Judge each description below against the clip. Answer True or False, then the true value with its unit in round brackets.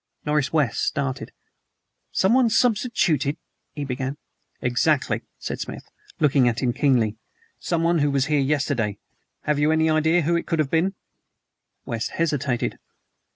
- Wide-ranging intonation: False (3.5 semitones)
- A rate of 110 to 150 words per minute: True (140 wpm)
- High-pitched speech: False (150 Hz)